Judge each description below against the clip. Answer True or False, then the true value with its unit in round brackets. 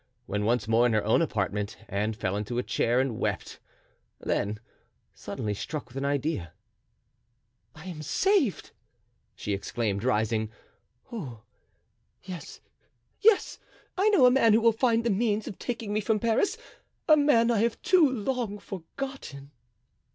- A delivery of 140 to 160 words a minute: True (150 wpm)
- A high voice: False (165 Hz)